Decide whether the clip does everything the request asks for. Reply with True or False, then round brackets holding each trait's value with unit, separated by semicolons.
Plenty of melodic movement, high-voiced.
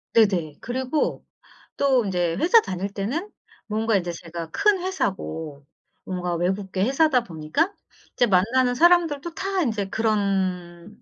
True (7.5 semitones; 210 Hz)